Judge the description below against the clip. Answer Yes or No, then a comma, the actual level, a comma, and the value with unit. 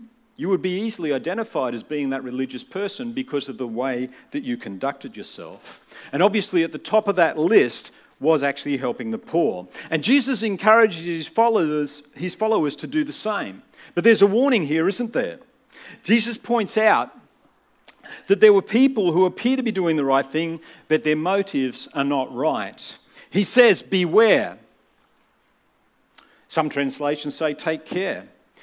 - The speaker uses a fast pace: No, average, 165 wpm